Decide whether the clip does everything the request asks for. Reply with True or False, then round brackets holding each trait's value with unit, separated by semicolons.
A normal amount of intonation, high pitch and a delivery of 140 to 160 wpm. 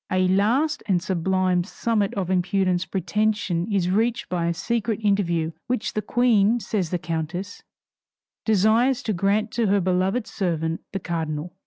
True (3.5 semitones; 195 Hz; 150 wpm)